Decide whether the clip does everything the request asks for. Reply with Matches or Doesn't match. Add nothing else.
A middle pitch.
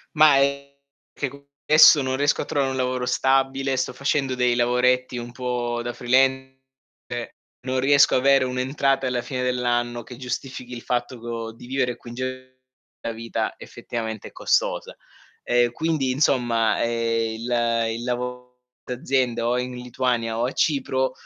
Doesn't match